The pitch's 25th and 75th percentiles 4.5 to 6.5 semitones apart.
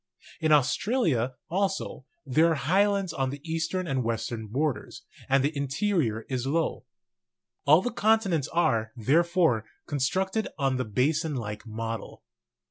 Yes: wide, 5.4 semitones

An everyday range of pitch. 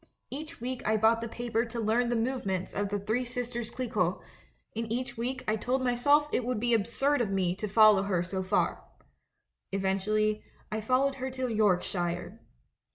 Yes: average, 3.5 semitones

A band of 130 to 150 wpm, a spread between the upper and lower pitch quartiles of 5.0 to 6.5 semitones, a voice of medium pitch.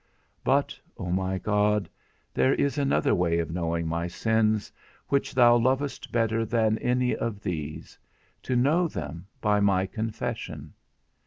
No: average, 140 wpm; average, 5.3 semitones; low, 105 Hz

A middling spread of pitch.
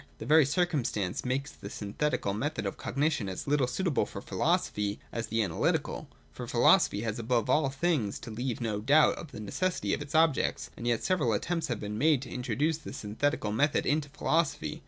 No: wide, 5.7 semitones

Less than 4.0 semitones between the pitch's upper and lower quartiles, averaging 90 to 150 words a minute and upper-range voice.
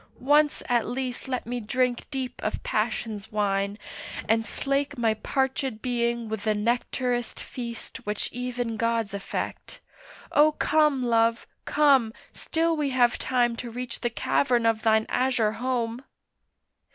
Yes: narrow, 2.5 semitones; average, 140 wpm; high, 240 Hz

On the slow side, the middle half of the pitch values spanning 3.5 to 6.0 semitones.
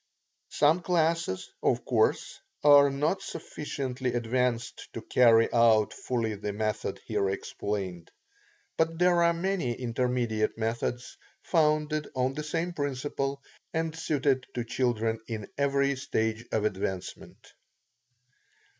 Yes: slow, 115 wpm; average, 5.1 semitones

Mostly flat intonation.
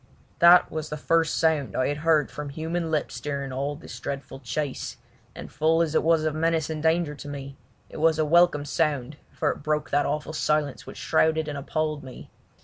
Yes: narrow, 1.8 semitones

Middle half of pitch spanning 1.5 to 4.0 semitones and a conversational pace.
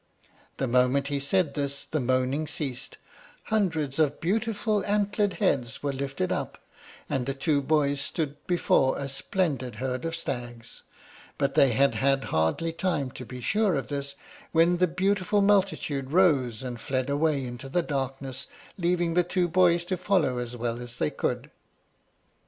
No: average, 5.1 semitones; average, 160 wpm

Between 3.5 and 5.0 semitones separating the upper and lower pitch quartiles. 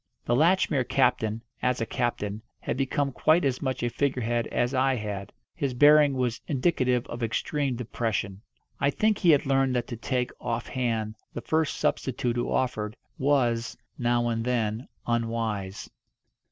No: average, 2.7 semitones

